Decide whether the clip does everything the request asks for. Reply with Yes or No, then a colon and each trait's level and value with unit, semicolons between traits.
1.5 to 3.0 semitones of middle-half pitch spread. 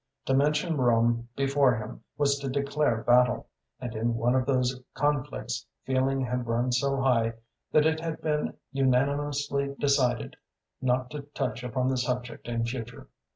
Yes: narrow, 2.5 semitones